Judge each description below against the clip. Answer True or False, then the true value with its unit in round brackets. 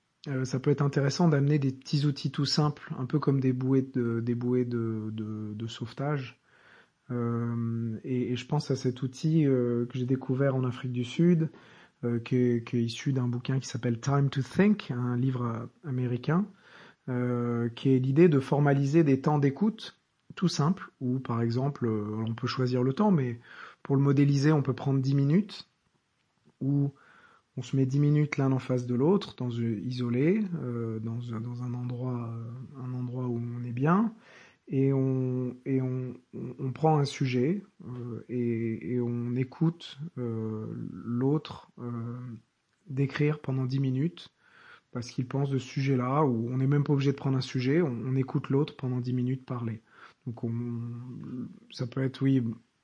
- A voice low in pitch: True (130 Hz)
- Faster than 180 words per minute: False (175 wpm)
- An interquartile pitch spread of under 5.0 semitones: True (2.8 semitones)